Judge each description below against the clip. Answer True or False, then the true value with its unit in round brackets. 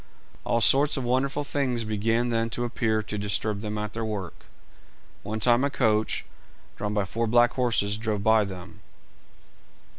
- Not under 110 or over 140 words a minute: False (160 wpm)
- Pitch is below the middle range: True (110 Hz)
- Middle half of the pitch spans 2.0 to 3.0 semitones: True (2.4 semitones)